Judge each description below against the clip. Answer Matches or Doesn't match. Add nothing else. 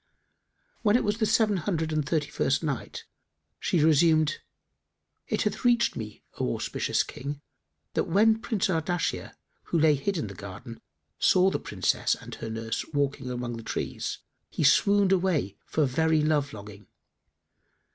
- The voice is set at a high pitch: Doesn't match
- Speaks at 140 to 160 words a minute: Matches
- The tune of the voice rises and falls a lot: Matches